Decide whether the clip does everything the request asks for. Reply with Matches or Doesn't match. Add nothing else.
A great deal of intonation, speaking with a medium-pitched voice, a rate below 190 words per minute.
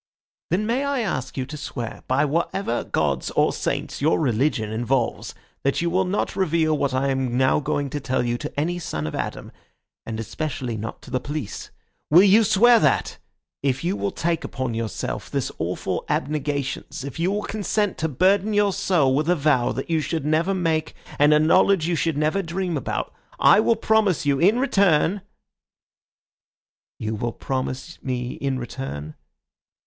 Matches